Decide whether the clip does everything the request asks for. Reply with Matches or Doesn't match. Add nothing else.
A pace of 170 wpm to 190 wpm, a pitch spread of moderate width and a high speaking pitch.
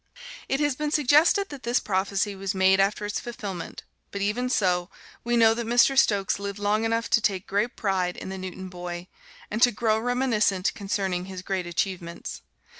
Matches